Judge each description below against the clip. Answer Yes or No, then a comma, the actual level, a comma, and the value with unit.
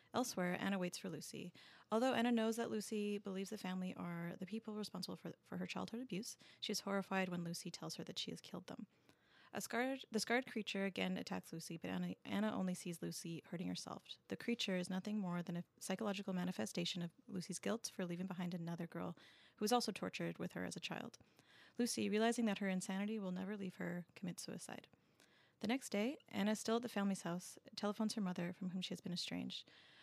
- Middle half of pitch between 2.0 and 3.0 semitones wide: No, average, 3.5 semitones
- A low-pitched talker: No, high, 195 Hz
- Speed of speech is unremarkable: No, fast, 210 wpm